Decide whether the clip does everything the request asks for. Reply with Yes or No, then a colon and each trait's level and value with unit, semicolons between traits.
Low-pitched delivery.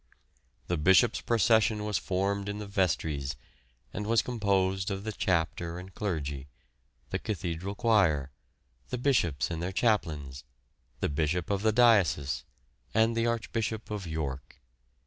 Yes: very low, 95 Hz